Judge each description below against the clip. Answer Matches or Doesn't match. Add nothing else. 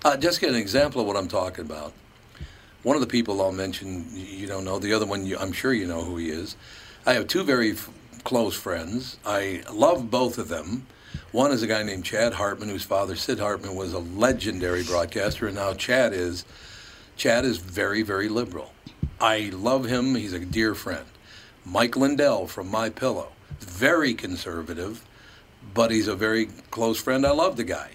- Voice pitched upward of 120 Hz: Doesn't match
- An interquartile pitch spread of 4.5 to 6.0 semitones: Doesn't match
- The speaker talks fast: Doesn't match